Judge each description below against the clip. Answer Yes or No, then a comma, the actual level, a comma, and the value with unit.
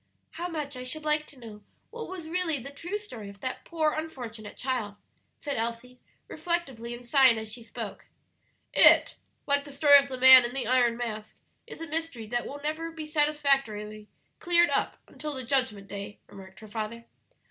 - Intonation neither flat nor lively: Yes, average, 5.0 semitones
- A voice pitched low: No, very high, 260 Hz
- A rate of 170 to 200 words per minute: Yes, average, 185 wpm